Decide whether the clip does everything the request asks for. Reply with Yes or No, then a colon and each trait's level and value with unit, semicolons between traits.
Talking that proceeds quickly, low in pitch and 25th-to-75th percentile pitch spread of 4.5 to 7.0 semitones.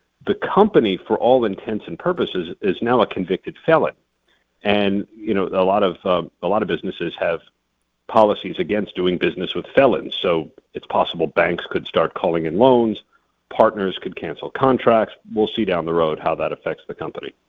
No: average, 180 wpm; low, 100 Hz; average, 4.9 semitones